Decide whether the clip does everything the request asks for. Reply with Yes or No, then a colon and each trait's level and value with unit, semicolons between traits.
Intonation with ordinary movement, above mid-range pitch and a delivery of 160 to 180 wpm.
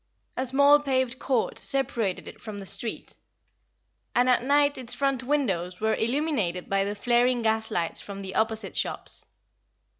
No: average, 4.5 semitones; high, 240 Hz; average, 150 wpm